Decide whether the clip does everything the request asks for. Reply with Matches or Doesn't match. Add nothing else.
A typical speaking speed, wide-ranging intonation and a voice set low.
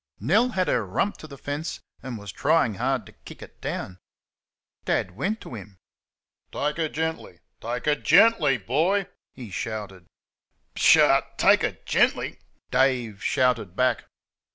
Matches